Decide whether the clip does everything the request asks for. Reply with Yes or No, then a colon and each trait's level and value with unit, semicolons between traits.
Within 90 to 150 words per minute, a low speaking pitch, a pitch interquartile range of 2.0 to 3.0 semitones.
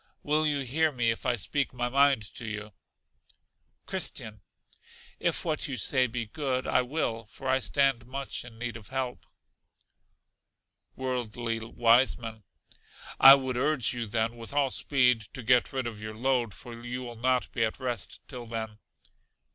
No: average, 165 wpm; low, 125 Hz; average, 2.7 semitones